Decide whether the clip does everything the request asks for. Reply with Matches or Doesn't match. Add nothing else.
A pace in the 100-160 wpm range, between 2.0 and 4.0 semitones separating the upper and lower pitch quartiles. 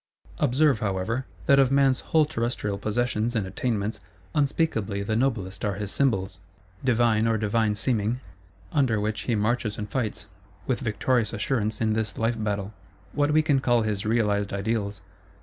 Matches